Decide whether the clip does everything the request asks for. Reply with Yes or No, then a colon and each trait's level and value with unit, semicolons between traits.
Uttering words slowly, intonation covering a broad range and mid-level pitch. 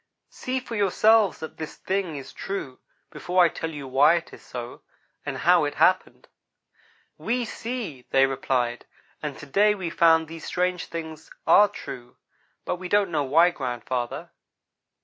No: average, 165 wpm; wide, 5.8 semitones; medium, 165 Hz